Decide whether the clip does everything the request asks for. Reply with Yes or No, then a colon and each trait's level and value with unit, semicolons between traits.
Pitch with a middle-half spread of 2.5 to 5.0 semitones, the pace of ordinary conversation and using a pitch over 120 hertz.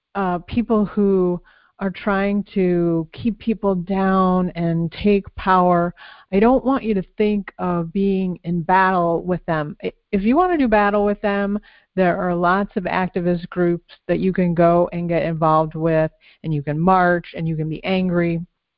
Yes: average, 2.9 semitones; average, 175 wpm; medium, 185 Hz